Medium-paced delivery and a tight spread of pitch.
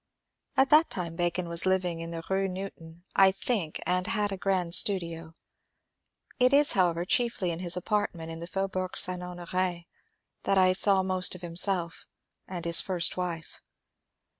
Yes: average, 165 wpm; narrow, 2.2 semitones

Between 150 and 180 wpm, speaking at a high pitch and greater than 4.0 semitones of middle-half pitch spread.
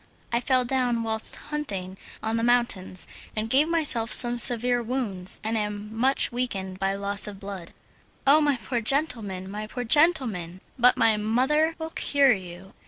Yes: average, 165 wpm; high, 230 Hz; average, 4.4 semitones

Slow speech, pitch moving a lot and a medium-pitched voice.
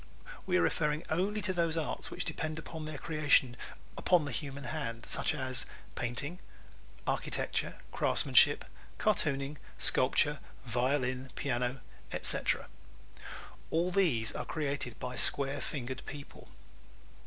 No: slow, 120 wpm; average, 3.7 semitones; medium, 145 Hz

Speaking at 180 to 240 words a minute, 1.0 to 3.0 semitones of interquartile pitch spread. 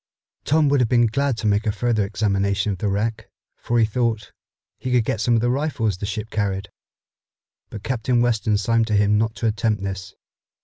Yes: fast, 205 wpm; narrow, 2.6 semitones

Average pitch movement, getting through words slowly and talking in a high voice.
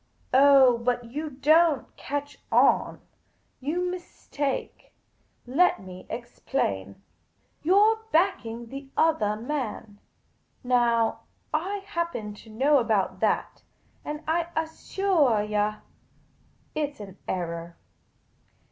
No: wide, 6.3 semitones; slow, 105 wpm; very high, 265 Hz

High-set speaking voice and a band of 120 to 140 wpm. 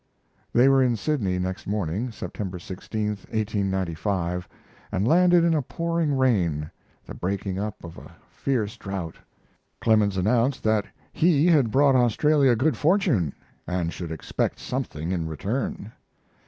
No: low, 105 Hz; slow, 135 wpm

